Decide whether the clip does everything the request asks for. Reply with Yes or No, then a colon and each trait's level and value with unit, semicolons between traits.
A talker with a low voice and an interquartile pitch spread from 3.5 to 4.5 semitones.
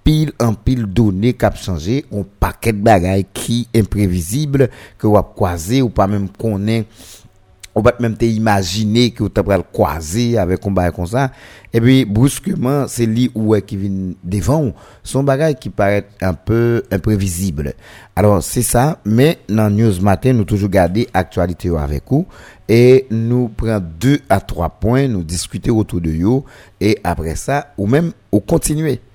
Yes: low, 110 Hz; average, 4.0 semitones